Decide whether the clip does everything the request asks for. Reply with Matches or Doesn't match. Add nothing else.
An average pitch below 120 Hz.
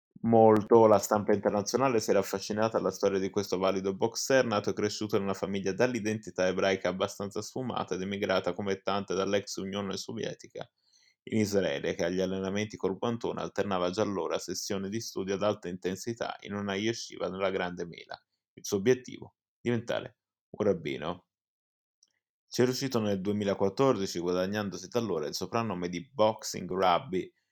Matches